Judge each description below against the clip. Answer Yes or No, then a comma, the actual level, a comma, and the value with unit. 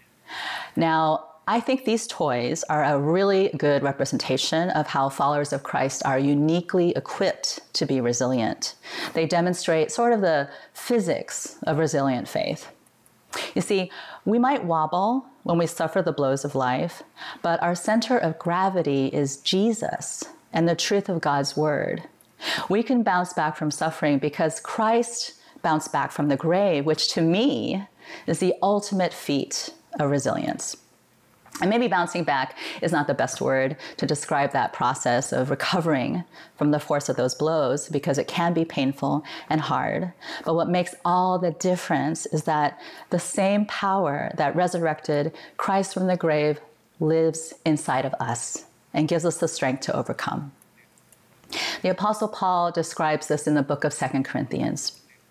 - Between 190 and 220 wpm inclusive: No, average, 155 wpm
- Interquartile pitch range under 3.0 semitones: No, average, 4.3 semitones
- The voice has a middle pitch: Yes, medium, 165 Hz